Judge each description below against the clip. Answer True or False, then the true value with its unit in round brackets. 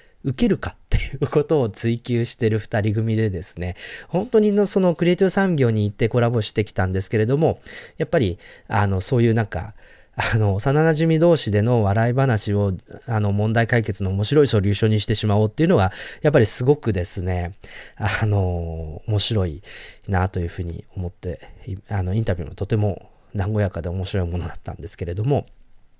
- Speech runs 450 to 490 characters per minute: False (390 characters per minute)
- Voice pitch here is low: True (110 Hz)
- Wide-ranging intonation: False (4.2 semitones)